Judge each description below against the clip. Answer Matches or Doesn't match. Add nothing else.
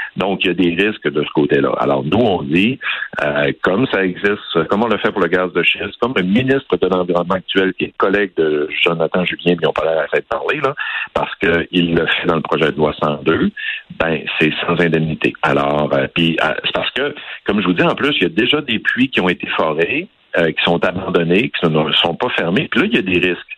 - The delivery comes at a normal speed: Doesn't match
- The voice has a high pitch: Doesn't match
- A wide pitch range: Doesn't match